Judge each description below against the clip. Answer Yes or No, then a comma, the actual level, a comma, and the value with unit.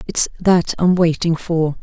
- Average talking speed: Yes, average, 165 wpm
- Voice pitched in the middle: Yes, medium, 170 Hz